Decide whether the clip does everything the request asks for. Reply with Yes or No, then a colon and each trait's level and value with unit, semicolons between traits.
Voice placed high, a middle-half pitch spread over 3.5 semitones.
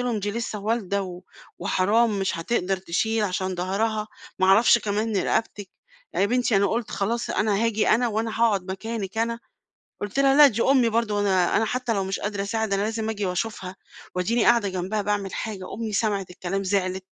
No: high, 210 Hz; average, 2.8 semitones